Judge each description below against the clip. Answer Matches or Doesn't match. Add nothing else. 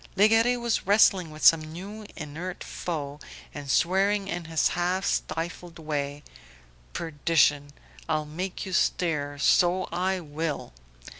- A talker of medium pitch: Matches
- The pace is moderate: Doesn't match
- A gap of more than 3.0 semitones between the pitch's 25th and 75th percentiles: Matches